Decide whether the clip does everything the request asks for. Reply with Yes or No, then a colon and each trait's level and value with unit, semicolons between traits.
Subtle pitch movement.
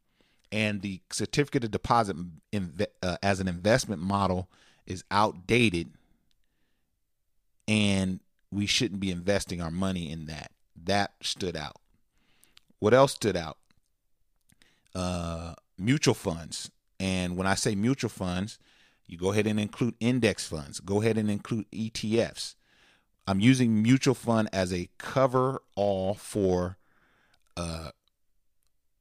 No: average, 3.5 semitones